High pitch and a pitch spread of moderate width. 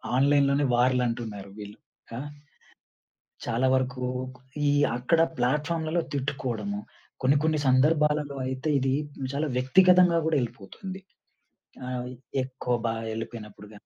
No: low, 130 Hz; average, 3.7 semitones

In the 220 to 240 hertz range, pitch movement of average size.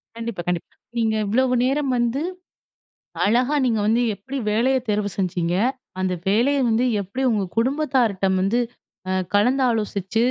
Yes: high, 225 Hz; average, 4.2 semitones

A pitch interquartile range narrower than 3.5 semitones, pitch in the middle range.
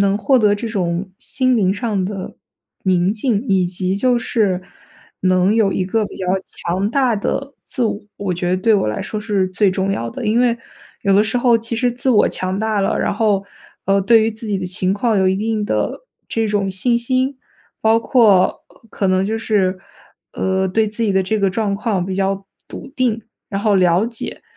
No: average, 3.1 semitones; high, 205 Hz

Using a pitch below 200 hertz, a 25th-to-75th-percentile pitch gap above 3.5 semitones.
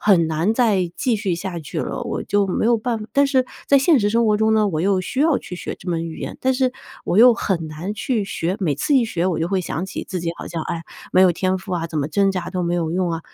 Yes: high, 190 Hz; average, 4.7 semitones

